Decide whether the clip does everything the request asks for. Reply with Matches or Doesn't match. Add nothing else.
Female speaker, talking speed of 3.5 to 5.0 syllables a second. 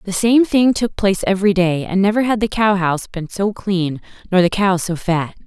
Doesn't match